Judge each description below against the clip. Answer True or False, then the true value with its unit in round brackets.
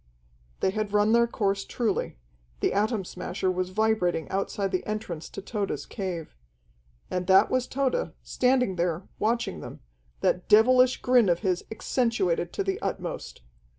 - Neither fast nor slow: True (150 wpm)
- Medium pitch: False (200 Hz)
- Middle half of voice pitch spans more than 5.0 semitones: False (3.9 semitones)